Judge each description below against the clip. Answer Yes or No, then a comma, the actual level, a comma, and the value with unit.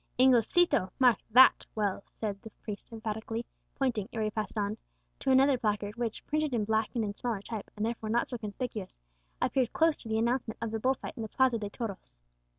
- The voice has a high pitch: Yes, high, 225 Hz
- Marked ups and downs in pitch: No, average, 3.0 semitones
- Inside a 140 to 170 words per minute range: No, fast, 205 wpm